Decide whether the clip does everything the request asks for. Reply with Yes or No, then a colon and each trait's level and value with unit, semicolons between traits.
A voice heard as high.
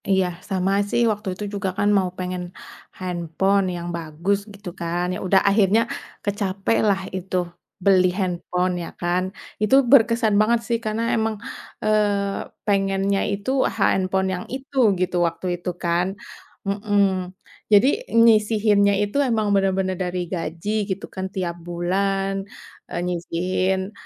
Yes: high, 195 Hz